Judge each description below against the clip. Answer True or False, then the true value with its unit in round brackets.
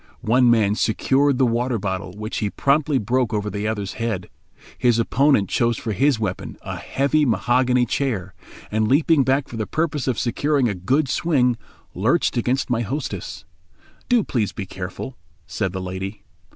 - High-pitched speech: False (120 Hz)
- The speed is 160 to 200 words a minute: True (165 wpm)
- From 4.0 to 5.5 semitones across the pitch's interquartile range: True (4.6 semitones)